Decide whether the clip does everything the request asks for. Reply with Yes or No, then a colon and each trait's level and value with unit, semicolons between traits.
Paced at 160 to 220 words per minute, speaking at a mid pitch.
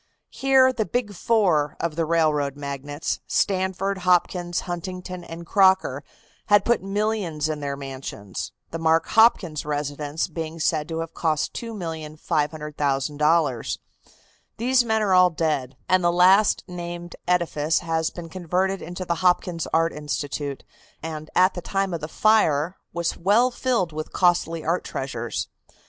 No: average, 140 wpm; medium, 170 Hz